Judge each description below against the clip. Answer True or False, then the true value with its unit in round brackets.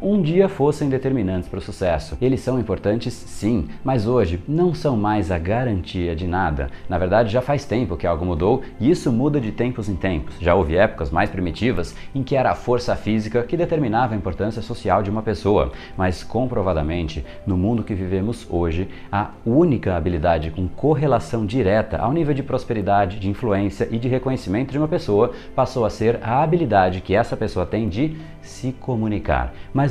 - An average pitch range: False (5.7 semitones)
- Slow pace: False (185 wpm)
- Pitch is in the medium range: False (105 Hz)